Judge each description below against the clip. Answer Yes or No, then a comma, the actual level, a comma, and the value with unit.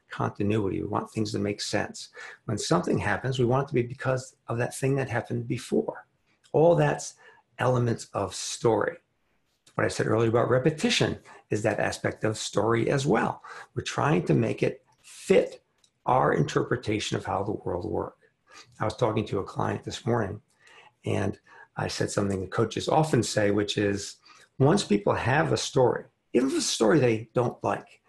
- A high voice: No, low, 115 Hz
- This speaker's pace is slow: No, average, 180 wpm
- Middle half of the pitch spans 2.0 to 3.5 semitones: No, average, 3.9 semitones